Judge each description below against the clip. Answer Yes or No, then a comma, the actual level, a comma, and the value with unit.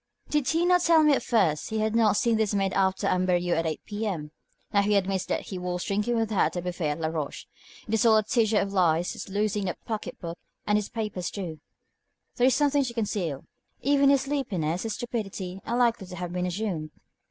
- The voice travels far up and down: No, average, 4.2 semitones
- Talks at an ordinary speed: No, fast, 220 wpm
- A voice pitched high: Yes, high, 205 Hz